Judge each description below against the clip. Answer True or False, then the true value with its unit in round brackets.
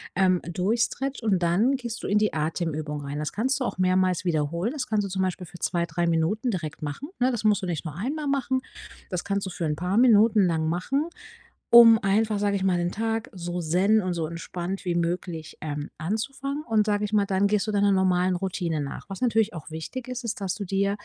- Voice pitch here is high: True (195 Hz)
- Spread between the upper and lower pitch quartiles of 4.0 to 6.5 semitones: True (4.4 semitones)